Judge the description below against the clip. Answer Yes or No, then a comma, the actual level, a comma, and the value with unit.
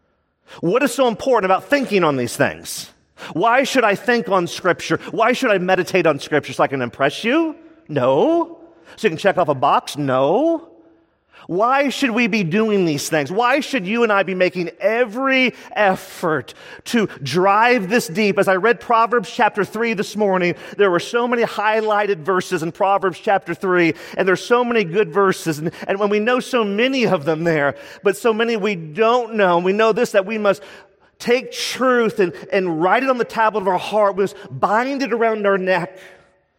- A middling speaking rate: Yes, average, 195 wpm